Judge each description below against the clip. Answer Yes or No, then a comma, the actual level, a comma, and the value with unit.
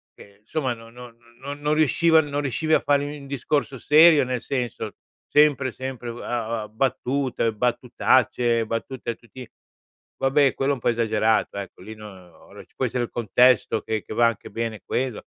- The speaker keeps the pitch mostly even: No, average, 3.5 semitones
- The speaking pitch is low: Yes, low, 125 Hz